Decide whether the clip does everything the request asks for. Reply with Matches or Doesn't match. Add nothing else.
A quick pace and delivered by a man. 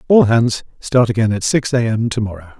Matches